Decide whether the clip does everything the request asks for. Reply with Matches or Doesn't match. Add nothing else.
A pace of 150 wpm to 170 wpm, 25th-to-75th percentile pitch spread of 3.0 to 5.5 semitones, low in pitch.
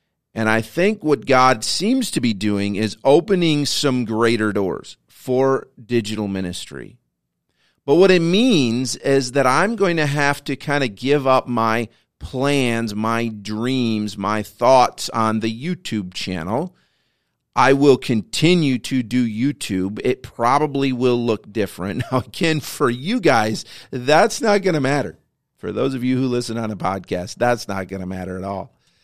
Matches